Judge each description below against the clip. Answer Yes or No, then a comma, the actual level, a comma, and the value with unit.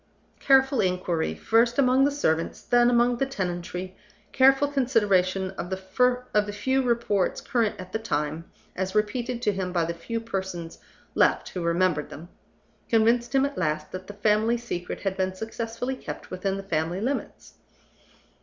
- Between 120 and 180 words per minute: Yes, average, 155 wpm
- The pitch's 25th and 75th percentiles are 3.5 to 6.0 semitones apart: Yes, average, 4.8 semitones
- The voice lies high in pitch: Yes, high, 205 Hz